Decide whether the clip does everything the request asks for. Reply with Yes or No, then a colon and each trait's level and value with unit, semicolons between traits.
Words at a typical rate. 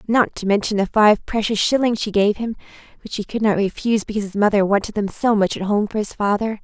No: fast, 245 wpm